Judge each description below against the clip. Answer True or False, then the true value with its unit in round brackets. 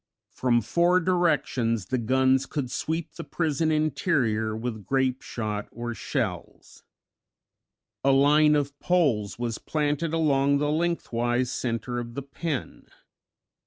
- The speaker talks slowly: True (120 wpm)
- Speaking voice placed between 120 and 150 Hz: True (135 Hz)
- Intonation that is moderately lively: True (4.5 semitones)